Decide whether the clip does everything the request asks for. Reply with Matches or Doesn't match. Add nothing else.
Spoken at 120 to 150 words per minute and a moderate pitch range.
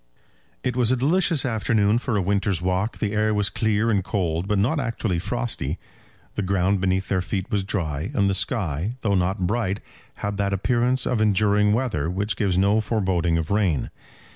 Doesn't match